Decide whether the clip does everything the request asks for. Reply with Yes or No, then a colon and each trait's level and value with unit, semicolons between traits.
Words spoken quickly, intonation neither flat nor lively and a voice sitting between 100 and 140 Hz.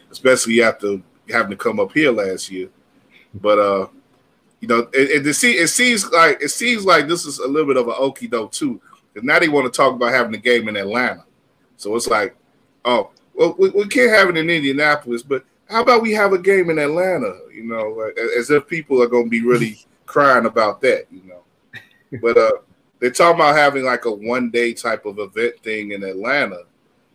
No: fast, 210 wpm; wide, 7.7 semitones; low, 135 Hz